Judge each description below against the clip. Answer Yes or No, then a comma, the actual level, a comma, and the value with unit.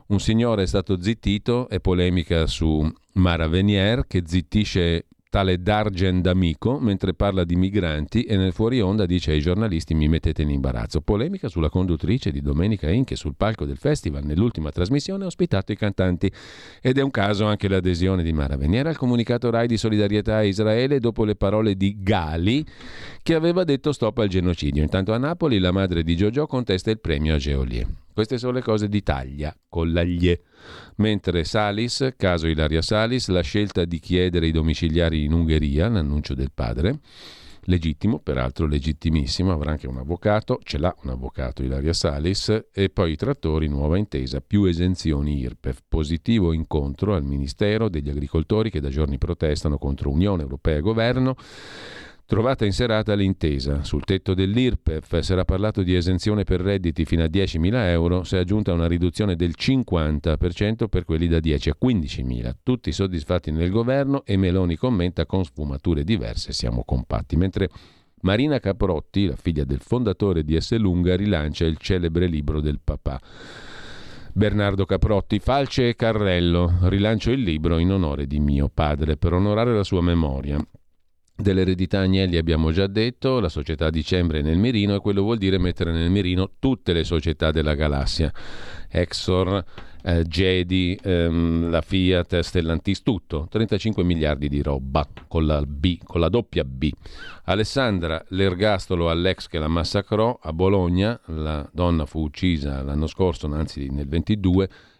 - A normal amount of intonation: Yes, average, 4.7 semitones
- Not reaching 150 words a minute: No, average, 160 wpm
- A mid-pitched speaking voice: No, very low, 90 Hz